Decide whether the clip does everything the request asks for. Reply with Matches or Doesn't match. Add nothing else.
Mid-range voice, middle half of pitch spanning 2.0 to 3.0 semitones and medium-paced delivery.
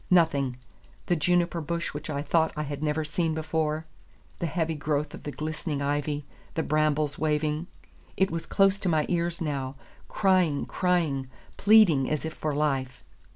Matches